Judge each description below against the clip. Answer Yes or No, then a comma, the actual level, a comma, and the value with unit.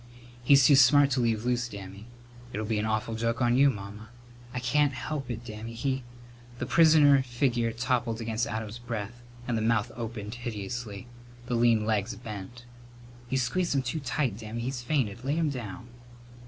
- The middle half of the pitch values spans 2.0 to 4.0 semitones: Yes, average, 2.8 semitones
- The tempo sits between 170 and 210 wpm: Yes, average, 180 wpm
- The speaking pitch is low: Yes, low, 120 Hz